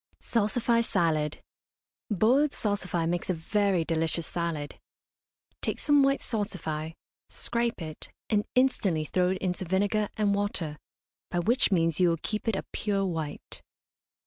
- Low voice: No, high, 190 Hz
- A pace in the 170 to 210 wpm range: No, average, 140 wpm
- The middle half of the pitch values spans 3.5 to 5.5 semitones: Yes, average, 4.6 semitones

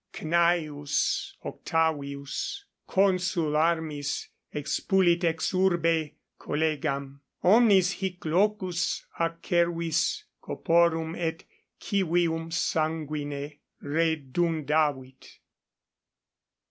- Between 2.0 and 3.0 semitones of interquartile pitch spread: Yes, average, 2.7 semitones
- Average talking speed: No, slow, 60 wpm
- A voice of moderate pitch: Yes, medium, 165 Hz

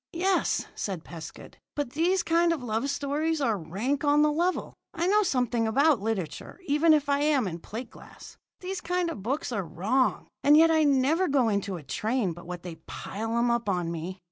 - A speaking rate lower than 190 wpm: No, average, 200 wpm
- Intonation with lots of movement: Yes, wide, 7.6 semitones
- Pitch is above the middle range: Yes, very high, 265 Hz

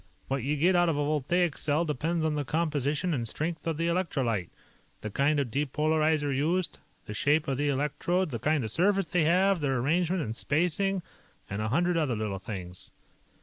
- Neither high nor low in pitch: Yes, medium, 150 Hz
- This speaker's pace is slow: No, average, 190 wpm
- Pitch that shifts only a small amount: No, average, 4.1 semitones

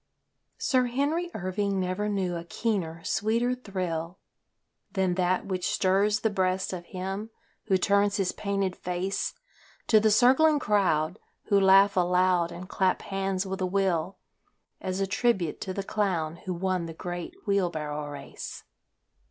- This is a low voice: No, high, 190 Hz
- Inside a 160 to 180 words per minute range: No, average, 150 wpm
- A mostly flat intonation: Yes, narrow, 2.3 semitones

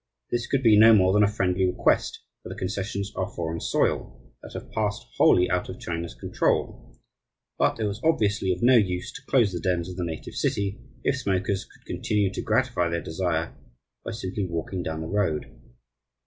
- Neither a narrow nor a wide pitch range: Yes, average, 3.0 semitones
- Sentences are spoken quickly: No, average, 190 wpm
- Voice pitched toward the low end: Yes, very low, 95 Hz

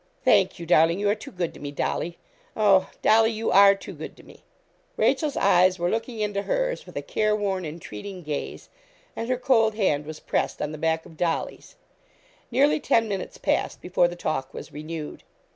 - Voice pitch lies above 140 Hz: Yes, high, 190 Hz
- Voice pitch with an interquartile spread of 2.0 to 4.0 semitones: No, average, 5.2 semitones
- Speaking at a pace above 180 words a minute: Yes, average, 190 wpm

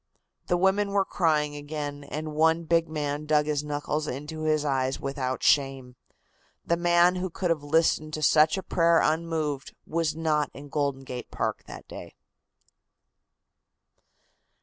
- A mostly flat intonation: Yes, narrow, 2.3 semitones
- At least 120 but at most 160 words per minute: Yes, average, 150 wpm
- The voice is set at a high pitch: No, medium, 155 Hz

